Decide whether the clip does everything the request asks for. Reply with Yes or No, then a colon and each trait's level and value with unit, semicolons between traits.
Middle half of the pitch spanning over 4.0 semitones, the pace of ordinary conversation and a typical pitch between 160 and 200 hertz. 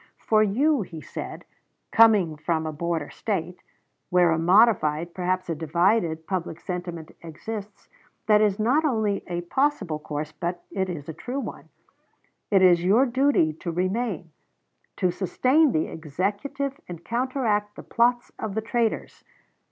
Yes: average, 5.2 semitones; average, 145 wpm; medium, 185 Hz